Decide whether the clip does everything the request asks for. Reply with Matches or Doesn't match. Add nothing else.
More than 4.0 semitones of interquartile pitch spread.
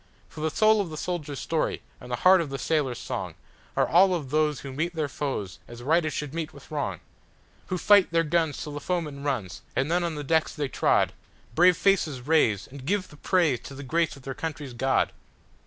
Doesn't match